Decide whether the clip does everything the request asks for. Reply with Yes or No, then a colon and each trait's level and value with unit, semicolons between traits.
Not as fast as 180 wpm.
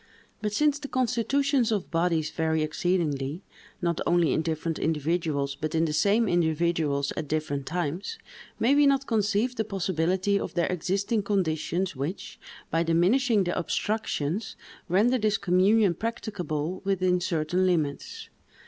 Yes: average, 140 wpm